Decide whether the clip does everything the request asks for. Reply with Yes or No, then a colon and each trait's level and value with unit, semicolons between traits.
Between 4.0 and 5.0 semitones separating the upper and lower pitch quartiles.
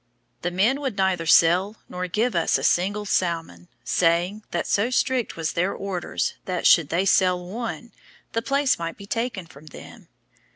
Yes: average, 4.6 semitones